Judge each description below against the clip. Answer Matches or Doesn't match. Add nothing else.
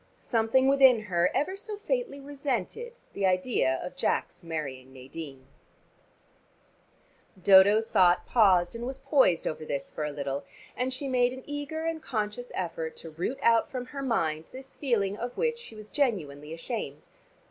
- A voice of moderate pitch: Doesn't match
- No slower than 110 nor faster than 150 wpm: Doesn't match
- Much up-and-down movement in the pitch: Matches